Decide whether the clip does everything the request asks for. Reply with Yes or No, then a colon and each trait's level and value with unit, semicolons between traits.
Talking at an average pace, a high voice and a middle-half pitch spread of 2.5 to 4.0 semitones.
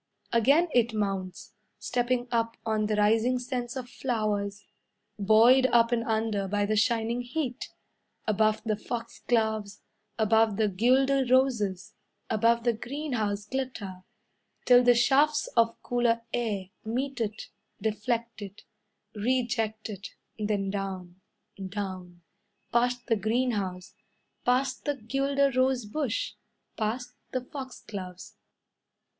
No: slow, 115 wpm; high, 230 Hz; average, 3.1 semitones